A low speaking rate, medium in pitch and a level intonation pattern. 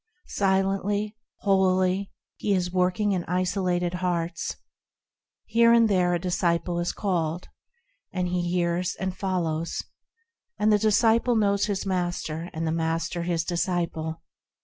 Yes: slow, 125 wpm; medium, 180 Hz; narrow, 2.3 semitones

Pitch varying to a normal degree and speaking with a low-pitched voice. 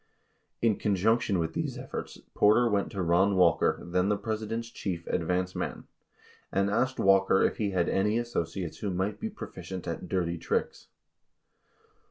Yes: average, 3.0 semitones; very low, 95 Hz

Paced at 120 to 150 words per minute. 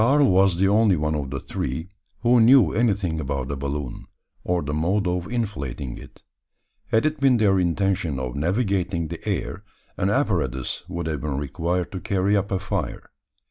No: average, 180 wpm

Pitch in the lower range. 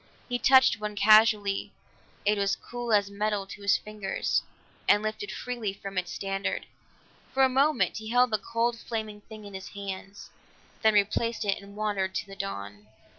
No: high, 210 Hz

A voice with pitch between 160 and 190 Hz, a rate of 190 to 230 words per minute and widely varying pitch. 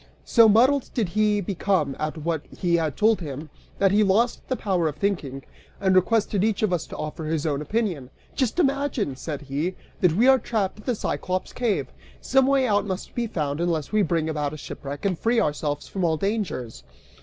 Yes: medium, 185 Hz; average, 200 wpm; wide, 6.0 semitones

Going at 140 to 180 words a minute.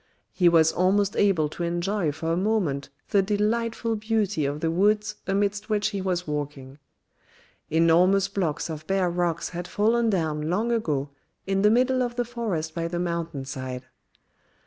Yes: average, 165 wpm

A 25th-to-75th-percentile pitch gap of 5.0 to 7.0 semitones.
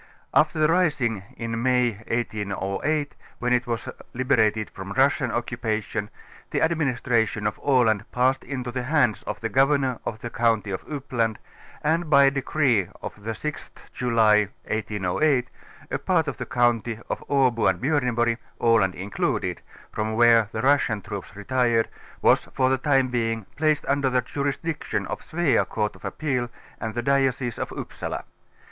No: average, 3.7 semitones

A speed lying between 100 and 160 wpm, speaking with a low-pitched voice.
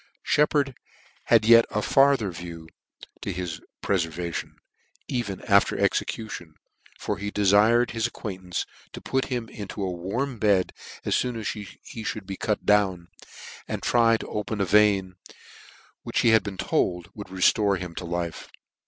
Yes: average, 155 wpm; low, 100 Hz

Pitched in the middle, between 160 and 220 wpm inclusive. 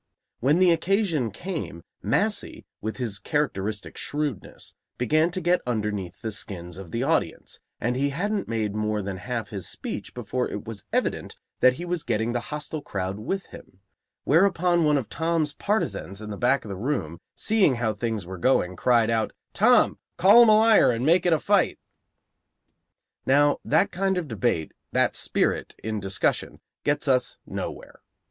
No: low, 125 Hz; average, 170 wpm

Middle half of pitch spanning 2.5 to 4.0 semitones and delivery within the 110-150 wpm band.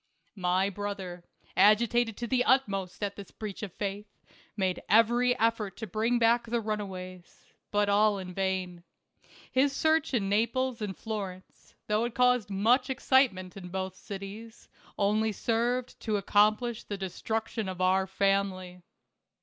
Yes: average, 3.3 semitones; average, 145 wpm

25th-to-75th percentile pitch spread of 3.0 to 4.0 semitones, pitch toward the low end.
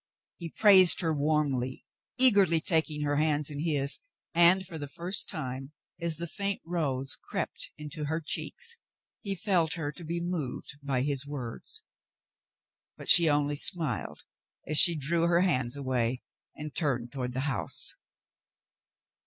No: average, 3.5 semitones; medium, 150 Hz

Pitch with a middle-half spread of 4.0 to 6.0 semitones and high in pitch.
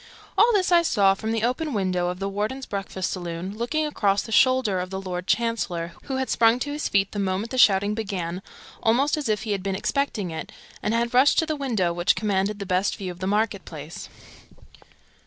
Yes: average, 4.5 semitones; high, 205 Hz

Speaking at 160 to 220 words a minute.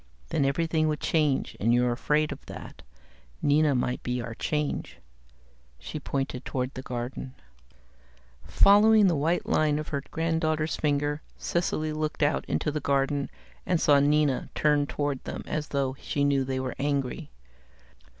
No: average, 150 wpm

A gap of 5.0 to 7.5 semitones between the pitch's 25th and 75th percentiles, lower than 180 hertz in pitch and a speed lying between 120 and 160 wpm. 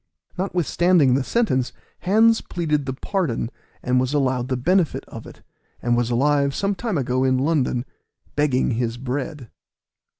Yes: wide, 5.5 semitones; medium, 140 Hz; average, 145 wpm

